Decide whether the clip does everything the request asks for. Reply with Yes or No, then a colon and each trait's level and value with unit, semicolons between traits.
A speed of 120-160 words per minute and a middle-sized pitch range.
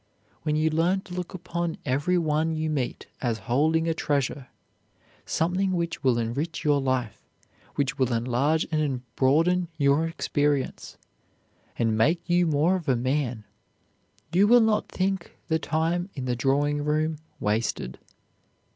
Yes: average, 145 wpm; average, 4.4 semitones